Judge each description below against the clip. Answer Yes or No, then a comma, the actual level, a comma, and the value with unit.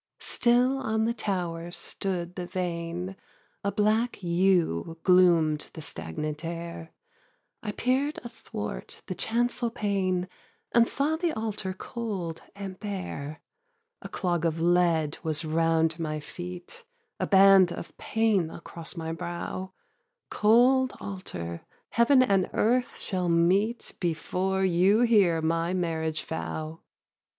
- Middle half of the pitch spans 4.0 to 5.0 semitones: Yes, average, 4.4 semitones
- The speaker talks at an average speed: No, slow, 125 wpm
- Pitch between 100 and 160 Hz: No, medium, 180 Hz